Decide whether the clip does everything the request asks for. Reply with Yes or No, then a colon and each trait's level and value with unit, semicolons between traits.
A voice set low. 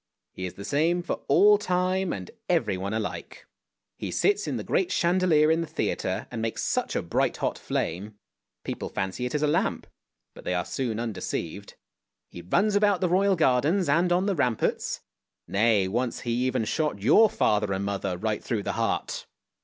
Yes: low, 130 Hz